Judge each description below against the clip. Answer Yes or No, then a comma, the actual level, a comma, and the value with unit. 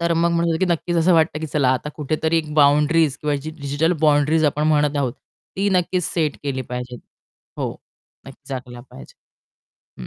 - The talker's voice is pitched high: No, medium, 150 Hz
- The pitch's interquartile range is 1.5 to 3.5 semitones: Yes, narrow, 2.5 semitones